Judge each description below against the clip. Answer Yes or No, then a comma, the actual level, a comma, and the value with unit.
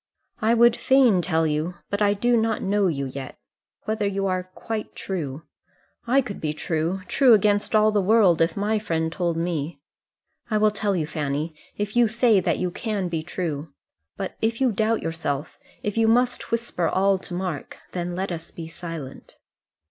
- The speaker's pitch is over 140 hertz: Yes, high, 190 Hz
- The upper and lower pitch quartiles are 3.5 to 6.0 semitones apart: Yes, average, 4.8 semitones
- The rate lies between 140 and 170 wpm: No, average, 185 wpm